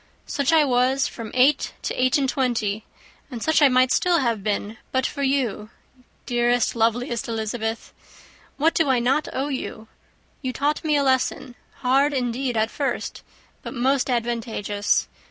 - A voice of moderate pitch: No, very high, 255 Hz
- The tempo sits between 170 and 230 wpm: No, average, 155 wpm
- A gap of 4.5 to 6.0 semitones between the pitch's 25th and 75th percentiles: No, average, 3.0 semitones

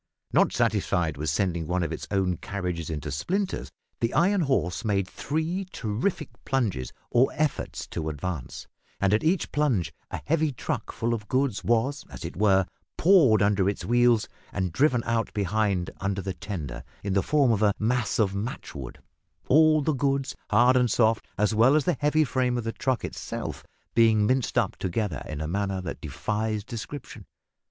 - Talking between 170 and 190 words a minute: Yes, average, 175 wpm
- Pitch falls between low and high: No, low, 110 Hz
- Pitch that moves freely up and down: Yes, wide, 5.7 semitones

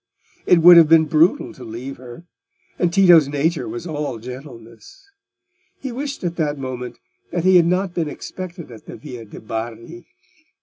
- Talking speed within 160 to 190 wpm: Yes, average, 170 wpm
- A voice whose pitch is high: No, medium, 155 Hz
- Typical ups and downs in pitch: No, wide, 5.9 semitones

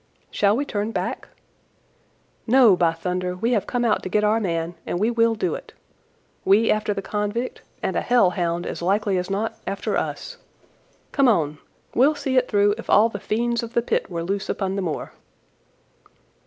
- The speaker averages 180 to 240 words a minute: Yes, average, 190 wpm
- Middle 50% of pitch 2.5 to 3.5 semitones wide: No, average, 4.1 semitones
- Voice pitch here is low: No, high, 205 Hz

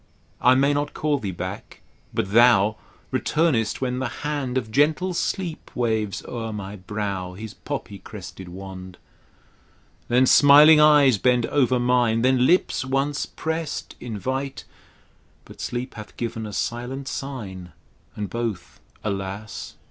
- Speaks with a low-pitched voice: Yes, low, 120 Hz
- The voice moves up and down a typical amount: Yes, average, 4.9 semitones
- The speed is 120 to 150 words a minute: Yes, slow, 135 wpm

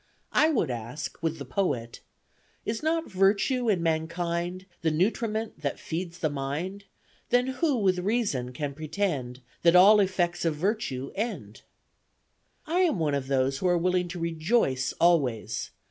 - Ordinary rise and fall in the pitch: No, wide, 5.9 semitones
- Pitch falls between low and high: Yes, medium, 175 Hz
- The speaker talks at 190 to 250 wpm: No, average, 150 wpm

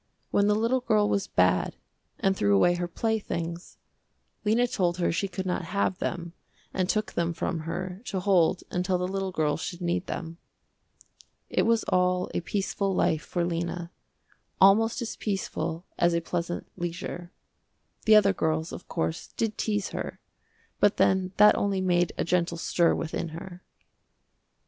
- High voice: No, medium, 180 Hz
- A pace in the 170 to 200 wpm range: No, average, 160 wpm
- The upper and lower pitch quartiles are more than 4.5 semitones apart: No, narrow, 2.6 semitones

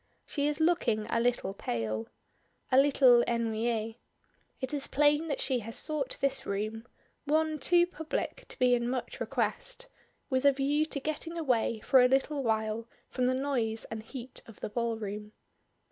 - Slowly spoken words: No, average, 165 wpm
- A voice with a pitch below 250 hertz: No, very high, 255 Hz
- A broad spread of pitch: No, average, 4.4 semitones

